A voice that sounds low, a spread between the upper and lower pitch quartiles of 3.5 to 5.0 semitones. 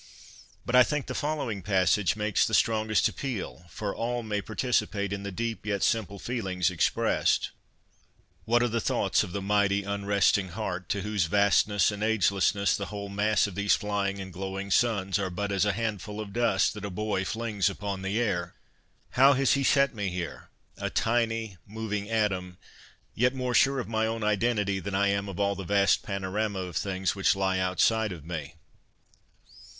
No: low, 100 Hz; narrow, 2.5 semitones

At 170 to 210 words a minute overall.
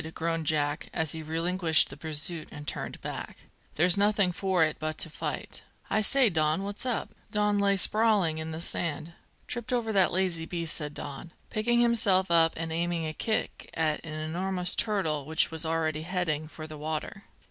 Yes: average, 180 wpm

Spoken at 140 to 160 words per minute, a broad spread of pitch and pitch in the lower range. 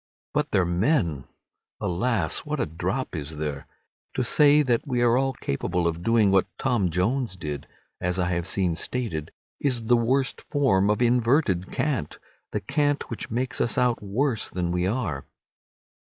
Yes: average, 155 wpm; wide, 6.4 semitones; low, 110 Hz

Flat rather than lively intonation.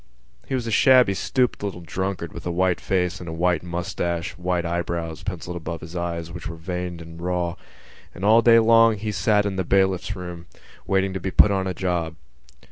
Yes: narrow, 2.3 semitones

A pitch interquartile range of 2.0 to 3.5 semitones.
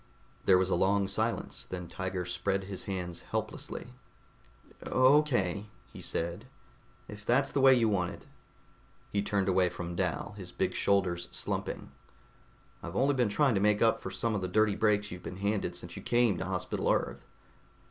Yes: average, 3.0 semitones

